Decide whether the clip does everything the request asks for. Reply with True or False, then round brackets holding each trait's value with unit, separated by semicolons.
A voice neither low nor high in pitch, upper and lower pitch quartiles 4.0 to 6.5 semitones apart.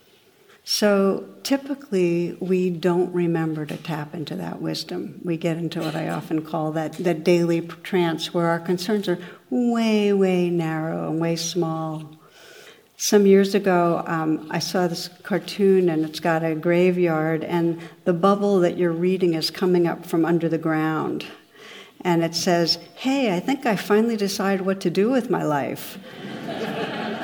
False (175 Hz; 2.9 semitones)